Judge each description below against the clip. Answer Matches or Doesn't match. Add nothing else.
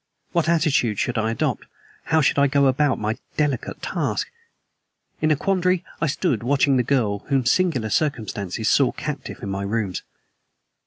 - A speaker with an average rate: Matches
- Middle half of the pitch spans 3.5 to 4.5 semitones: Doesn't match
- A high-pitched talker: Doesn't match